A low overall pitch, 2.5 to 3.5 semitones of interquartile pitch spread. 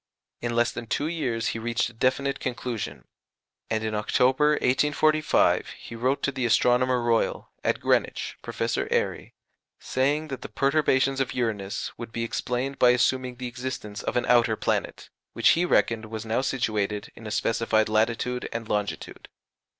Yes: low, 120 Hz; average, 2.8 semitones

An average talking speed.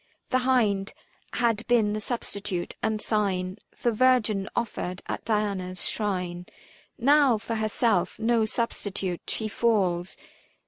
No: slow, 120 wpm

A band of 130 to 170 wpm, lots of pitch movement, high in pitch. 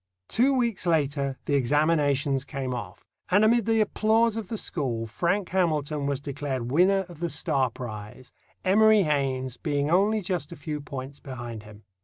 No: average, 165 wpm; wide, 6.3 semitones; medium, 150 Hz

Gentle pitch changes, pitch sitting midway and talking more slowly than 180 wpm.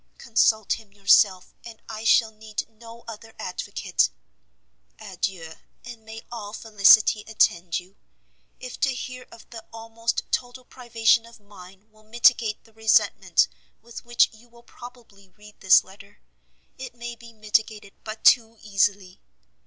No: narrow, 2.2 semitones; high, 220 Hz; average, 140 wpm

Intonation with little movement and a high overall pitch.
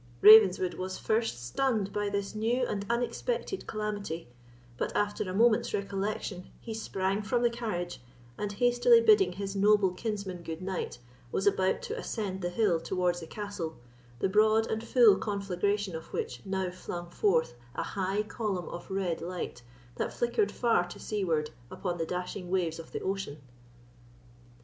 No: average, 3.2 semitones; high, 195 Hz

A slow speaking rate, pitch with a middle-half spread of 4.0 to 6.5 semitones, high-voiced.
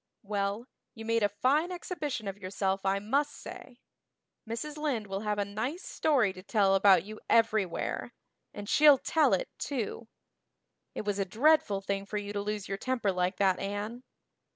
No: average, 175 wpm; average, 4.5 semitones; high, 210 Hz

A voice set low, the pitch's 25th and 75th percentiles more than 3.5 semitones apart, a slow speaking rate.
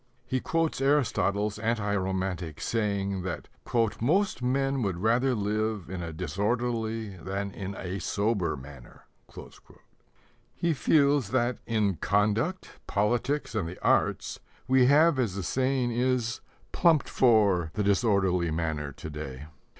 Yes: low, 105 Hz; average, 5.1 semitones; slow, 125 wpm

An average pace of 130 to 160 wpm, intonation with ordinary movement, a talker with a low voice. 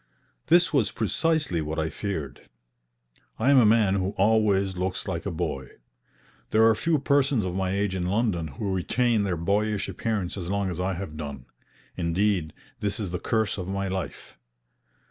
No: average, 175 wpm; average, 3.5 semitones; low, 100 Hz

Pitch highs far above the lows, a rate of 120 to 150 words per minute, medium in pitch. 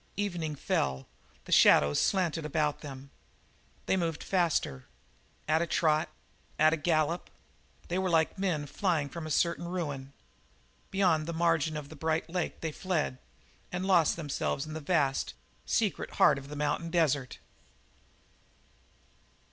No: average, 2.8 semitones; average, 140 wpm; medium, 160 Hz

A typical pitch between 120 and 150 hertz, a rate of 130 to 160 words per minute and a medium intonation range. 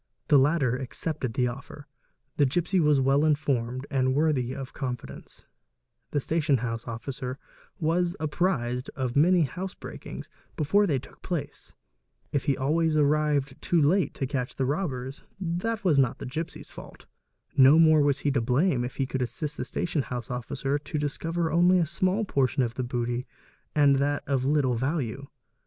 No: medium, 140 Hz; average, 170 wpm; average, 3.7 semitones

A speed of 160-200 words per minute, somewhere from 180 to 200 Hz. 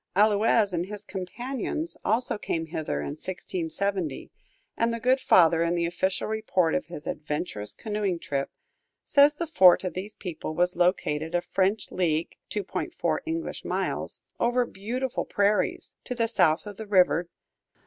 No: average, 150 wpm; high, 190 Hz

